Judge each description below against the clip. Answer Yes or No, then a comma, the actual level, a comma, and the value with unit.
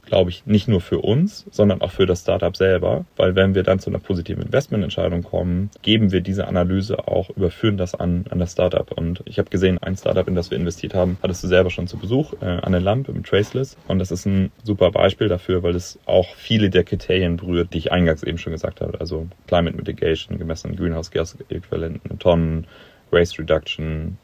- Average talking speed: No, fast, 215 wpm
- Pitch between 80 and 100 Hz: Yes, very low, 95 Hz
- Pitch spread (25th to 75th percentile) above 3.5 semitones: No, average, 2.7 semitones